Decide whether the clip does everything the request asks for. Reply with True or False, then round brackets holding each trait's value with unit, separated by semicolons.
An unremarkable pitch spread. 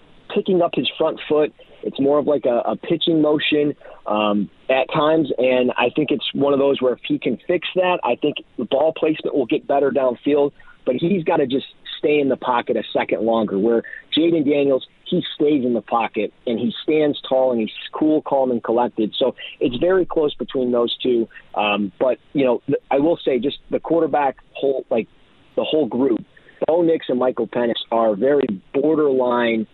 True (4.3 semitones)